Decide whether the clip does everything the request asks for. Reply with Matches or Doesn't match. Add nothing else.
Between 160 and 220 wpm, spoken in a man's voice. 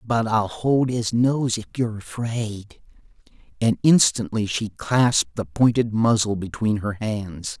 Doesn't match